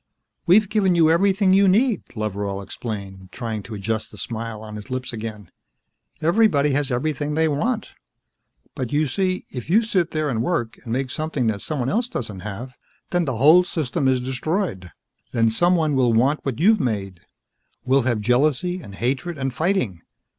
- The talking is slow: No, average, 175 wpm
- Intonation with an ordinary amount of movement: No, wide, 7.4 semitones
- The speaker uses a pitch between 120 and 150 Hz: Yes, low, 135 Hz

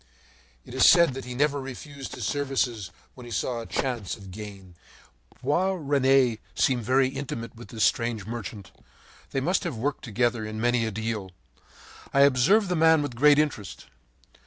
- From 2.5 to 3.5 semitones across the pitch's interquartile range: No, average, 4.1 semitones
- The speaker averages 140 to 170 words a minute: Yes, average, 165 wpm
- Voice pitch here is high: No, low, 125 Hz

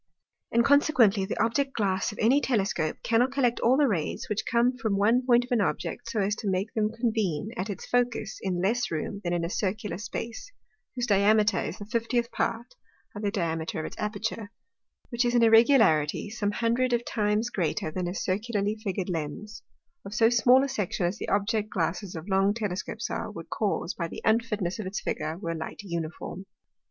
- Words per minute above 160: Yes, average, 195 wpm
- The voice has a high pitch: Yes, high, 210 Hz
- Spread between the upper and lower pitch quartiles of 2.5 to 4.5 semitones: Yes, average, 3.6 semitones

